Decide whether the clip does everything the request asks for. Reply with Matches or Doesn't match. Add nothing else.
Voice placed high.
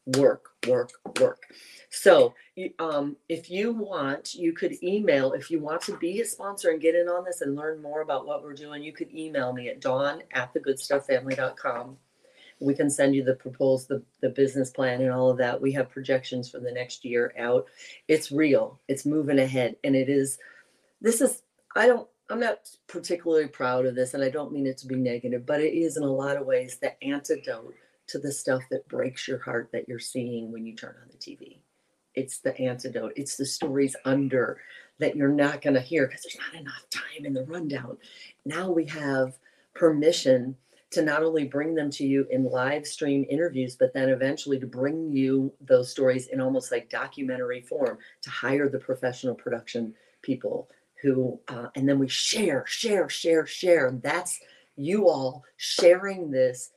Doesn't match